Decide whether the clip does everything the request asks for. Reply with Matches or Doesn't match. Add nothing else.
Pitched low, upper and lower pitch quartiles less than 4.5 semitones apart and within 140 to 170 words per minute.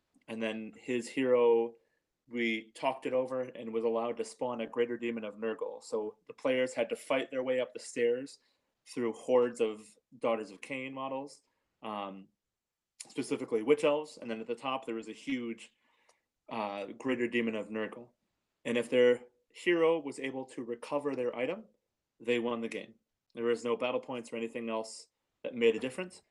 Doesn't match